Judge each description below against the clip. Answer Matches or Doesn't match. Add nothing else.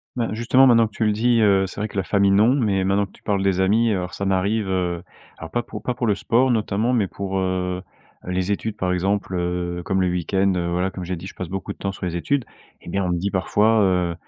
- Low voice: Matches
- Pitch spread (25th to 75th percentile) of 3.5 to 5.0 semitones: Doesn't match